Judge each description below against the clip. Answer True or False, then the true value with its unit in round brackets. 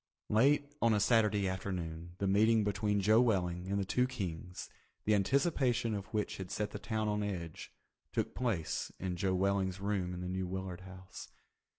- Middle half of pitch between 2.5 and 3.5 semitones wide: True (2.8 semitones)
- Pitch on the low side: True (100 Hz)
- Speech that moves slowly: False (180 wpm)